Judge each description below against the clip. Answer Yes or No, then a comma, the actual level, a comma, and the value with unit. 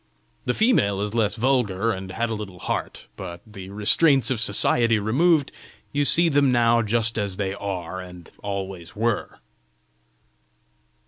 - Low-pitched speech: Yes, low, 105 Hz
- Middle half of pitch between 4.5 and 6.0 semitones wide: No, average, 3.7 semitones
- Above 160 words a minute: No, average, 145 wpm